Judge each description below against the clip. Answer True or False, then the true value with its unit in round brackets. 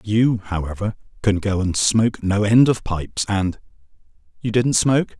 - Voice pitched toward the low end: True (105 Hz)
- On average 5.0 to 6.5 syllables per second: False (4.7 syllables/s)